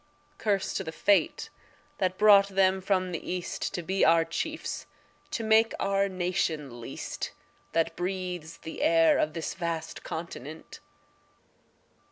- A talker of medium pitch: Yes, medium, 180 Hz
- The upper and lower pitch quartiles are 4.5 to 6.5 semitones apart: No, average, 3.0 semitones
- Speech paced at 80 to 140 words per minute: Yes, slow, 135 wpm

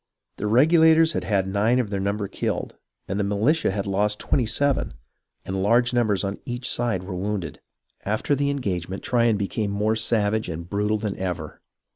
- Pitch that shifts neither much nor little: Yes, average, 3.5 semitones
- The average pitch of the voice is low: Yes, low, 105 Hz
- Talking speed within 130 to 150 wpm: No, average, 175 wpm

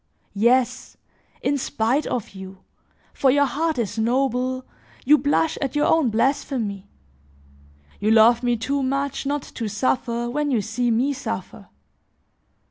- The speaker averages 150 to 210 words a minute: No, slow, 135 wpm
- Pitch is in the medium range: No, very high, 255 Hz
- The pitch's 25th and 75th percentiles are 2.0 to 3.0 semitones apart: No, average, 3.7 semitones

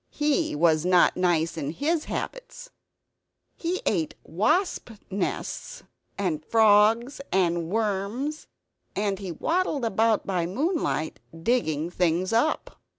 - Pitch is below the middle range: No, high, 205 Hz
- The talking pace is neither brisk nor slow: No, slow, 110 wpm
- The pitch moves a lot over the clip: Yes, wide, 8.8 semitones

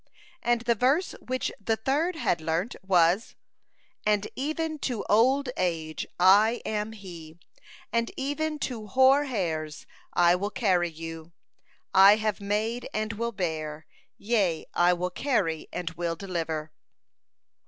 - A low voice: No, high, 205 Hz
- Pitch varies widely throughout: Yes, wide, 5.9 semitones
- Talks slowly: Yes, slow, 130 wpm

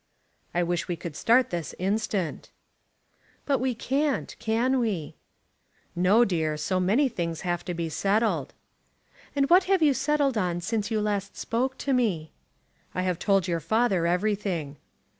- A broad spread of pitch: Yes, wide, 5.9 semitones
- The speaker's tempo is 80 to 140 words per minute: No, average, 155 wpm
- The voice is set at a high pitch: Yes, high, 200 Hz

